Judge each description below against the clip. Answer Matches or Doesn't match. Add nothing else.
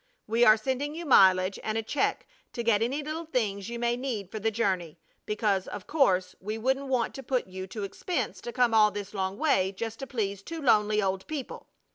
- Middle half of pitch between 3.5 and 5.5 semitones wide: Matches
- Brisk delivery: Matches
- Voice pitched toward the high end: Matches